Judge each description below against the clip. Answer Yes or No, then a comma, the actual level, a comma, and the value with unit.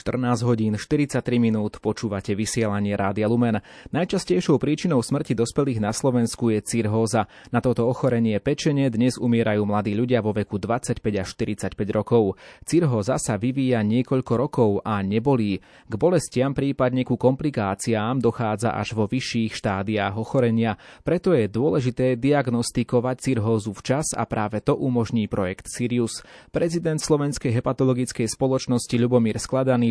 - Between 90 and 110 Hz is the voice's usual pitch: No, low, 120 Hz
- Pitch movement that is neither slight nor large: Yes, average, 3.3 semitones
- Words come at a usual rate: Yes, average, 130 wpm